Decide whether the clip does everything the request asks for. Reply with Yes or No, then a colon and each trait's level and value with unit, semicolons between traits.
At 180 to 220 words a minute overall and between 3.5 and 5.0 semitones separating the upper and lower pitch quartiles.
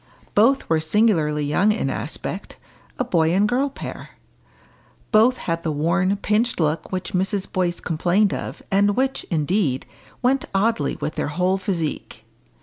No: average, 145 wpm; average, 4.6 semitones